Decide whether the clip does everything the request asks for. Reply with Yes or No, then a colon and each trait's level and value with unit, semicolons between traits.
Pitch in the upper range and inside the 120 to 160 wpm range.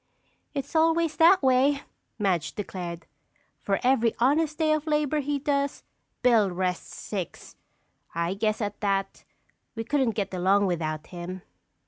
Yes: high, 225 Hz; slow, 135 wpm